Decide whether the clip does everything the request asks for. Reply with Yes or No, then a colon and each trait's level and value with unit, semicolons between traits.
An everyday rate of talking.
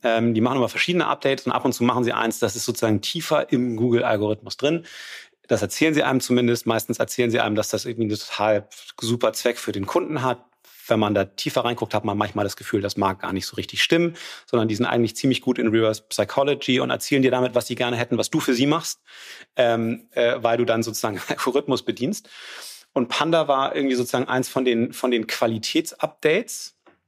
No: fast, 215 wpm